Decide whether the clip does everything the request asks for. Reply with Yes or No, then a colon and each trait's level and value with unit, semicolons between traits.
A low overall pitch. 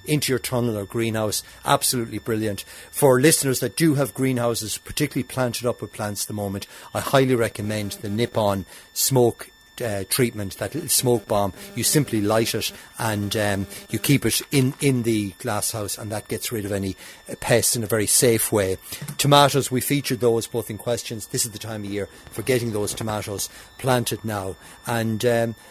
Yes: low, 115 Hz